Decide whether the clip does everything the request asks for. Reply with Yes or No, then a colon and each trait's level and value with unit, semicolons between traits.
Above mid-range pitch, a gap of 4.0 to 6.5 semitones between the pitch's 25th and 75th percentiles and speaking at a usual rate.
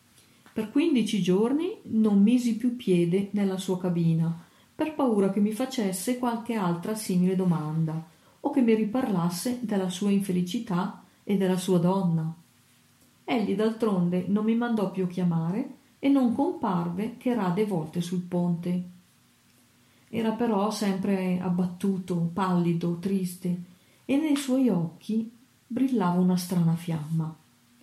Yes: high, 195 Hz; average, 4.3 semitones; average, 125 wpm